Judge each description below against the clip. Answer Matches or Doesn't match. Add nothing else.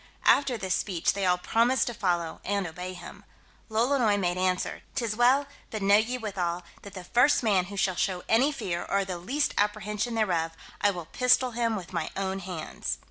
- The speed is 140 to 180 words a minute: Doesn't match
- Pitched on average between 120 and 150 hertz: Doesn't match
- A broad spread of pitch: Doesn't match